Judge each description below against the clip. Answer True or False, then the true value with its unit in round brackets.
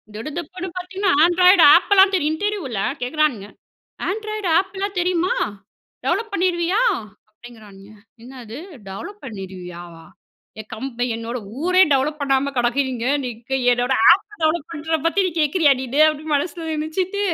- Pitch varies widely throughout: True (7.0 semitones)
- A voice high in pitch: True (305 Hz)